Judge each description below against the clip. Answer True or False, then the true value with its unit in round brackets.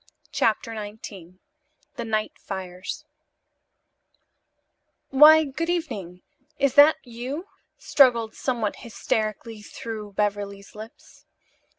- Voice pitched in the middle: False (225 Hz)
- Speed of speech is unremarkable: False (85 wpm)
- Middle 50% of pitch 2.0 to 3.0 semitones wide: False (4.6 semitones)